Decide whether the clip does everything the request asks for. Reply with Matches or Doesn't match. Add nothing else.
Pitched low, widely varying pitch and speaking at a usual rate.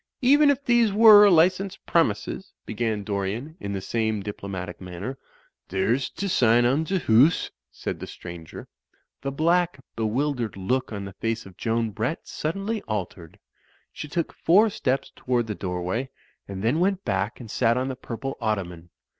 Matches